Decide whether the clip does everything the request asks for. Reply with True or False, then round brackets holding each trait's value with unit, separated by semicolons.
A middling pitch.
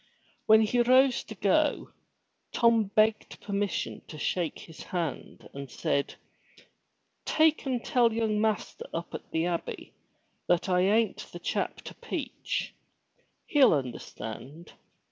False (205 Hz)